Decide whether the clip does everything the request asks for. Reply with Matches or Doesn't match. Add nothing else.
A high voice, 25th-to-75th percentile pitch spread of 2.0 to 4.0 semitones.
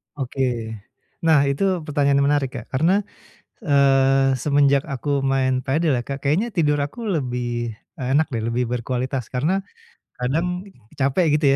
Doesn't match